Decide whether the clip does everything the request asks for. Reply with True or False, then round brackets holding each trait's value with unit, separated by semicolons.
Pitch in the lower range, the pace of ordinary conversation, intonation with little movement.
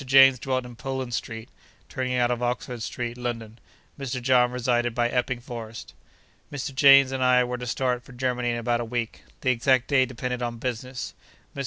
True (125 Hz; 190 wpm; 1.3 semitones)